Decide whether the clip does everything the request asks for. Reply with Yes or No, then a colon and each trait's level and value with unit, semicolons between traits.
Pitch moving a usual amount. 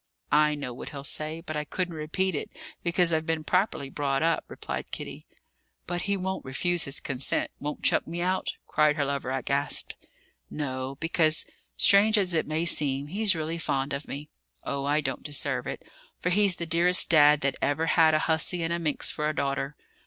Yes: average, 3.3 semitones